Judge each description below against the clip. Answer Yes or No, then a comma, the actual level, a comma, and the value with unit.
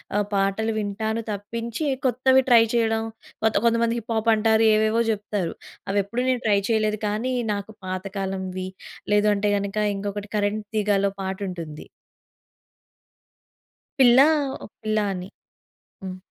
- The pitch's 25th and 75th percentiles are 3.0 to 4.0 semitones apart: No, narrow, 2.4 semitones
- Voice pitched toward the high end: Yes, high, 210 Hz